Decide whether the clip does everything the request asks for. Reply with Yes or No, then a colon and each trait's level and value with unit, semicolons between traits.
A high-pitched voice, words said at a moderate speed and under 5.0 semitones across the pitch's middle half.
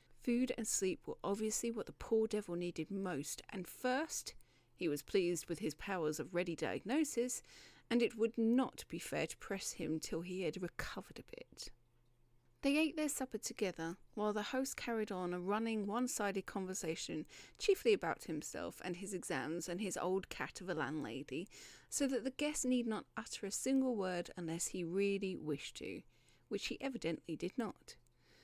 No: high, 200 Hz; average, 180 wpm; wide, 5.5 semitones